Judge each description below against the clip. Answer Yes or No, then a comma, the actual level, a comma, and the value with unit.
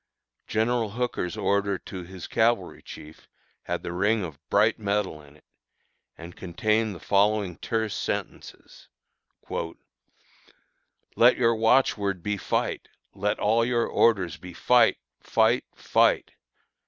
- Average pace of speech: No, slow, 125 wpm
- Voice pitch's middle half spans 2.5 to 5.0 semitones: Yes, average, 3.7 semitones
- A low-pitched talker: Yes, low, 105 Hz